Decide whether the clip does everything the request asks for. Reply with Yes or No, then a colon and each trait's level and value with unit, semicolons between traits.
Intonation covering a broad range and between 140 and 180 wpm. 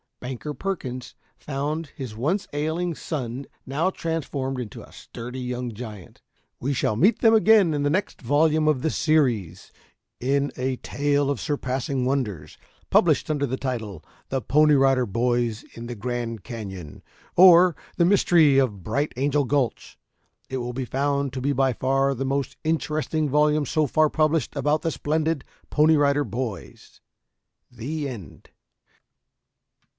No: average, 3.8 semitones; average, 150 wpm